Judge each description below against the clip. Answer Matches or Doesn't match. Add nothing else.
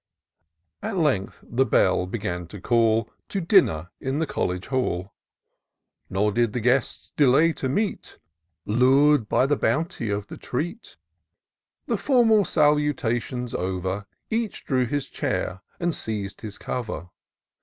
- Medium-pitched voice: Doesn't match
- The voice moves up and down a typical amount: Doesn't match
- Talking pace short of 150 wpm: Matches